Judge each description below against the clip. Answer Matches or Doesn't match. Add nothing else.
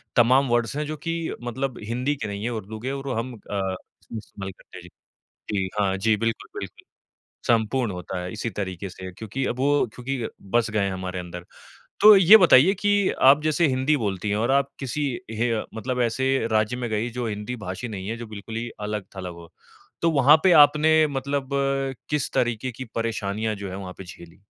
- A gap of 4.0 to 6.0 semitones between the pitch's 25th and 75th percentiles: Matches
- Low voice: Matches